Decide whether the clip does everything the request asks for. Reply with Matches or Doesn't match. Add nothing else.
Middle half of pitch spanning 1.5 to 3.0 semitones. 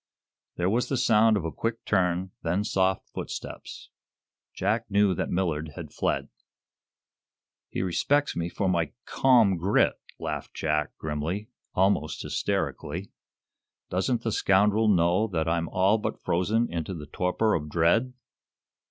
Doesn't match